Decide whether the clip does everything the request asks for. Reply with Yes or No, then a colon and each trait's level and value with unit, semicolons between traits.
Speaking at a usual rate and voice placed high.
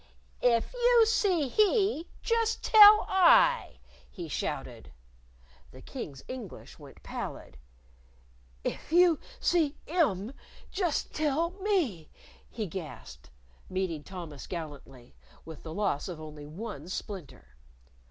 No: slow, 110 wpm; high, 230 Hz